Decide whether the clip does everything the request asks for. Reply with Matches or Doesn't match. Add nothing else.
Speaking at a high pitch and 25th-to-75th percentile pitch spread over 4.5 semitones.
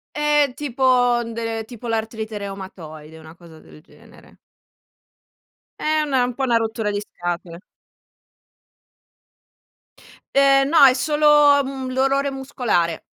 Matches